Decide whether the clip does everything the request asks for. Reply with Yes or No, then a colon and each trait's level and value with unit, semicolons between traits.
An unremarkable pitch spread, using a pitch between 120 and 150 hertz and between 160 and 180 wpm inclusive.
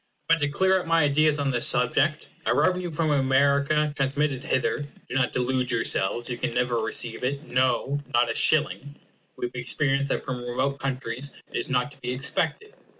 No: average, 3.0 semitones; low, 135 Hz; average, 190 wpm